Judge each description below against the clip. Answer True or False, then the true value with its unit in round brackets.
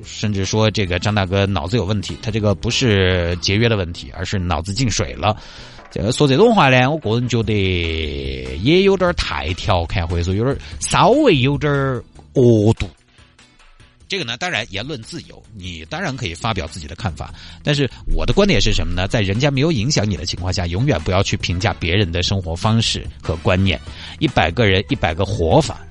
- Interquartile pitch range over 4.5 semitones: True (5.1 semitones)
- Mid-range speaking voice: False (100 Hz)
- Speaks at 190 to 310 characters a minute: True (290 characters per minute)